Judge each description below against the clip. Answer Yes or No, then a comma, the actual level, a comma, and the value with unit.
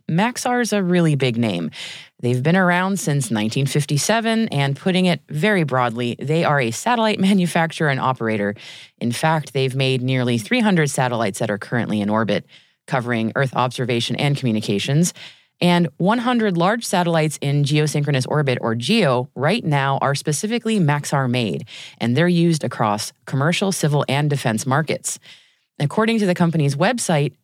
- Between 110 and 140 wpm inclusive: No, average, 150 wpm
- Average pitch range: No, wide, 5.8 semitones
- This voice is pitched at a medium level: Yes, medium, 145 Hz